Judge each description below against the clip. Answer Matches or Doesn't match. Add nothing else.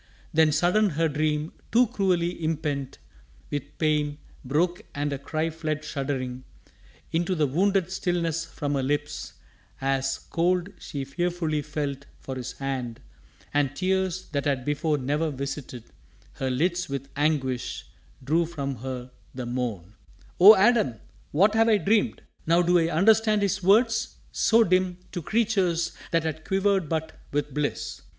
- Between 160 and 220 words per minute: Doesn't match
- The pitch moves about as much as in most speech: Matches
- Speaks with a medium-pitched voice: Matches